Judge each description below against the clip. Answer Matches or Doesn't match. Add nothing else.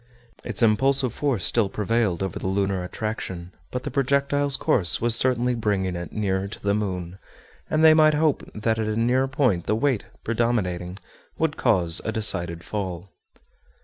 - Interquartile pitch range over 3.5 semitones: Matches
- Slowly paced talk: Doesn't match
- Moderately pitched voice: Doesn't match